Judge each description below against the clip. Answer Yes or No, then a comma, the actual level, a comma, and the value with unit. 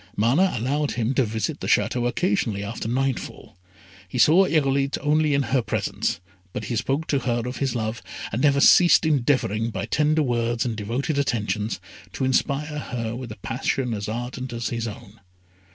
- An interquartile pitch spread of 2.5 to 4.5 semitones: Yes, average, 3.6 semitones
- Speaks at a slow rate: No, average, 175 wpm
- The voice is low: Yes, low, 125 Hz